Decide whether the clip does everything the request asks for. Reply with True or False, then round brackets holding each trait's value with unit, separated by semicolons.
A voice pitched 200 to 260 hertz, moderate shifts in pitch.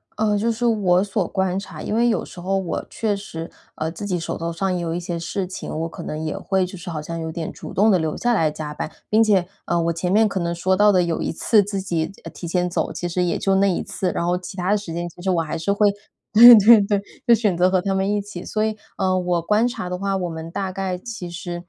False (185 Hz; 3.0 semitones)